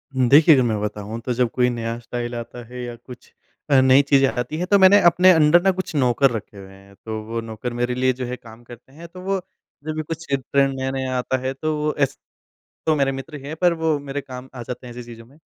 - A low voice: Yes, low, 130 Hz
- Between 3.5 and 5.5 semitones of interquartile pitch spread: Yes, average, 4.0 semitones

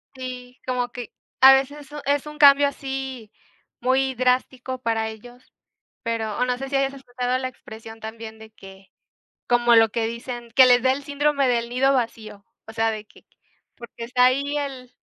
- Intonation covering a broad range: No, average, 2.7 semitones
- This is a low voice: No, very high, 250 Hz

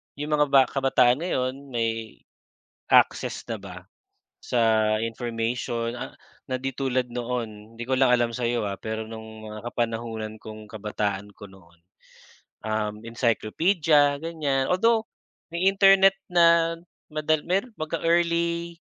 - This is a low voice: Yes, low, 125 Hz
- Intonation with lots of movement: Yes, wide, 6.1 semitones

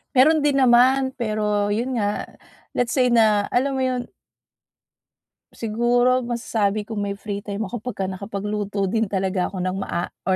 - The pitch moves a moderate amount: Yes, average, 3.5 semitones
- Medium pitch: No, high, 215 Hz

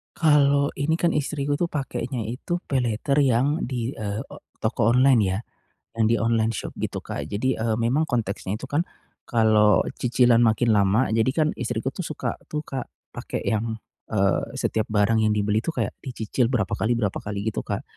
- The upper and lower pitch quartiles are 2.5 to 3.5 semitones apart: No, average, 4.1 semitones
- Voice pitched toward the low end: Yes, low, 115 Hz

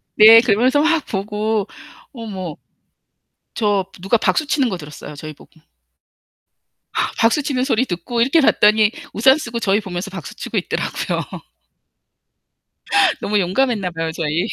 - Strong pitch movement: No, average, 4.7 semitones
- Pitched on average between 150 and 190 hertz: No, high, 215 Hz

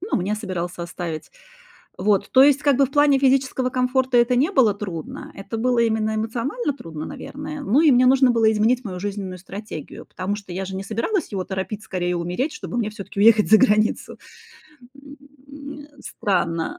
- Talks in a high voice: Yes, high, 220 Hz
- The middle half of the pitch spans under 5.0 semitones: No, wide, 5.4 semitones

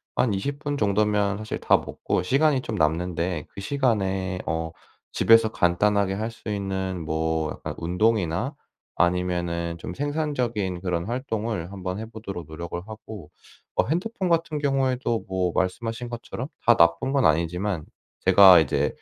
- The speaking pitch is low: Yes, low, 100 Hz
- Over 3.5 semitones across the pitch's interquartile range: Yes, average, 5.2 semitones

